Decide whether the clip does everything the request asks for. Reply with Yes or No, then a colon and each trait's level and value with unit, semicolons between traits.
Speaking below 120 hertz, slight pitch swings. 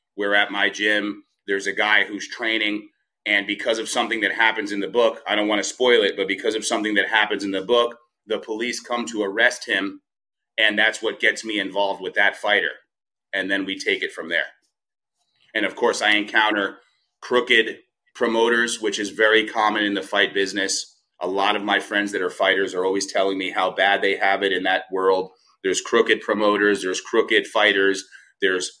Yes: low, 105 Hz; narrow, 2.0 semitones